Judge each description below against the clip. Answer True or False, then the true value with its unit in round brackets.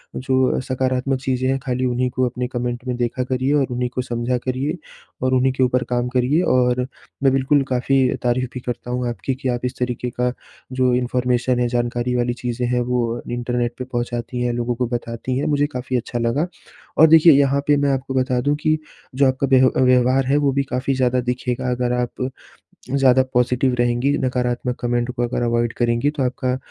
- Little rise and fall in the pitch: True (1.2 semitones)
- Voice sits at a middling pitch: False (125 Hz)